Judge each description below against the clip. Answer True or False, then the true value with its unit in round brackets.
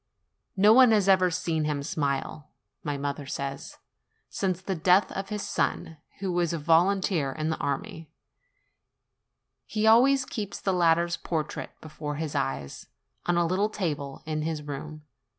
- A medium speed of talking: True (150 wpm)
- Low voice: False (165 Hz)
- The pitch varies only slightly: False (4.3 semitones)